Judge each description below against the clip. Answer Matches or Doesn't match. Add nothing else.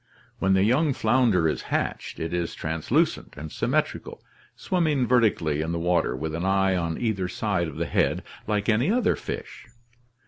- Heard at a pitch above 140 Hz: Doesn't match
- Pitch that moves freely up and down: Matches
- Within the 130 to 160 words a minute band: Doesn't match